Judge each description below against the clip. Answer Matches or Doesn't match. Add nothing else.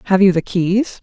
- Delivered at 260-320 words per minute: Doesn't match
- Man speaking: Doesn't match